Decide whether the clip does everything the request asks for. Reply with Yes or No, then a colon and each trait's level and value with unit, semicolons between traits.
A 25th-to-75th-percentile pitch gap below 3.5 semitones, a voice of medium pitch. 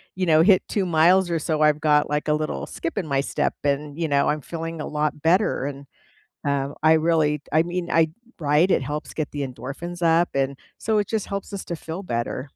Yes: average, 2.9 semitones; medium, 155 Hz